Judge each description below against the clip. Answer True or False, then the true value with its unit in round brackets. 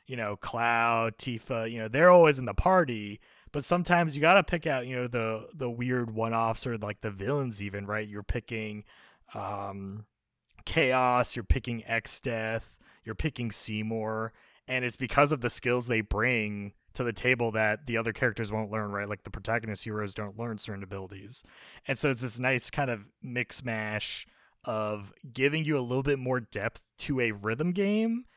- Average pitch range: True (3.2 semitones)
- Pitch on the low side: True (115 Hz)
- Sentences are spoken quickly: False (185 wpm)